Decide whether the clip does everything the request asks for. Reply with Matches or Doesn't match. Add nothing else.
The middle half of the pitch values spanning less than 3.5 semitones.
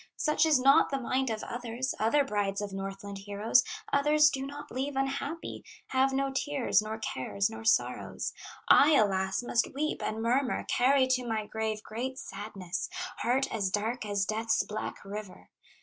Doesn't match